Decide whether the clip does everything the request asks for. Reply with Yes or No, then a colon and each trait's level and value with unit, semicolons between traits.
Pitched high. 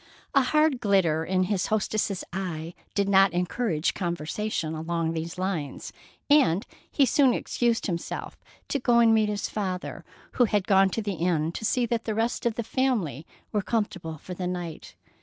Yes: high, 195 Hz